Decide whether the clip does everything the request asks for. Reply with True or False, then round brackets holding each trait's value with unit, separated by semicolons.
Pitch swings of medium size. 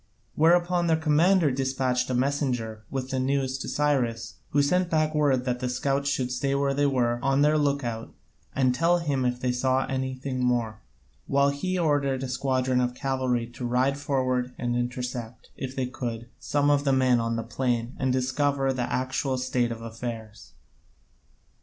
False (2.3 semitones)